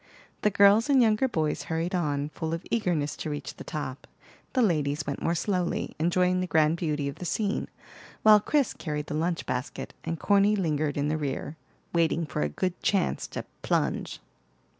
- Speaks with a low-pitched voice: No, medium, 165 Hz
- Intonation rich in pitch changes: No, average, 4.8 semitones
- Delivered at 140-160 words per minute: No, average, 185 wpm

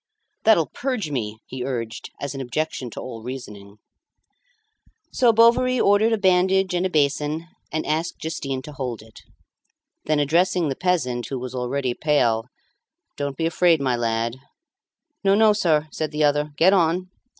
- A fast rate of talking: No, average, 160 wpm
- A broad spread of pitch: Yes, wide, 6.1 semitones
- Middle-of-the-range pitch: Yes, medium, 150 Hz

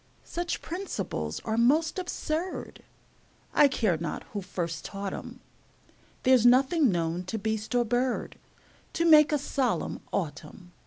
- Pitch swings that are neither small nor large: No, wide, 7.6 semitones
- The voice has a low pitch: No, high, 245 Hz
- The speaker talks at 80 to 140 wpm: Yes, slow, 135 wpm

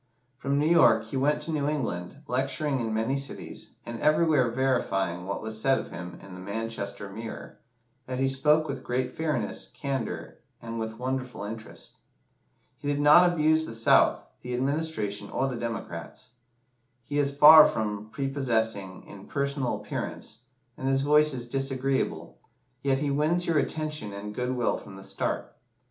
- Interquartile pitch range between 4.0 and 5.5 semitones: Yes, average, 4.5 semitones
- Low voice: Yes, low, 130 Hz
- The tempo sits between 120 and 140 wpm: No, average, 160 wpm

